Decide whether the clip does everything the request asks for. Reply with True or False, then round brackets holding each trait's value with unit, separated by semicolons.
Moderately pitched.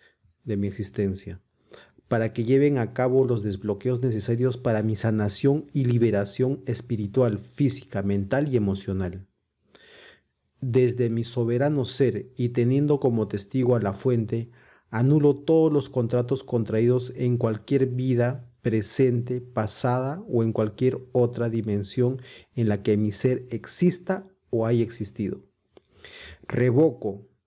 False (120 Hz)